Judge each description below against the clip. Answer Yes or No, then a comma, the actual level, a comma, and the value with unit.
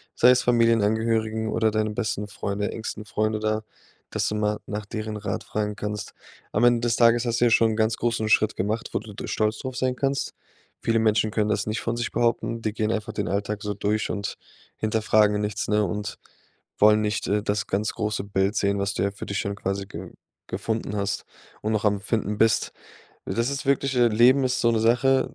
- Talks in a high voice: No, low, 110 Hz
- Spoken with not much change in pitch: Yes, narrow, 1.8 semitones